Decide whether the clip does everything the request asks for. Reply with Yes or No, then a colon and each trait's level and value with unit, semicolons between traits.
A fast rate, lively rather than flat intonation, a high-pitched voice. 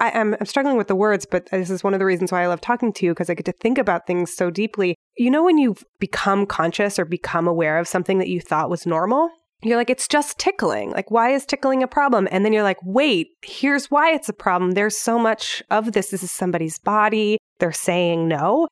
Yes: fast, 245 wpm; wide, 5.7 semitones; high, 205 Hz